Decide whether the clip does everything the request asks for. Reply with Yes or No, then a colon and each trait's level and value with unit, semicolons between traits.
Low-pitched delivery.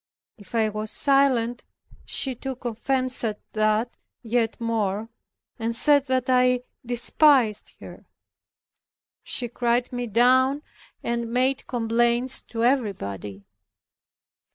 No: high, 240 Hz